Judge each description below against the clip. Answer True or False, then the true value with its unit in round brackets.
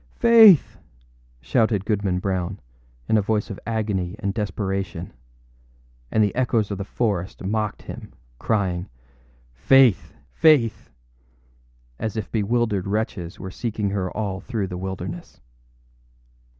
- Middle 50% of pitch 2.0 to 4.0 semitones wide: True (2.7 semitones)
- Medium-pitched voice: False (105 Hz)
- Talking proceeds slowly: True (120 wpm)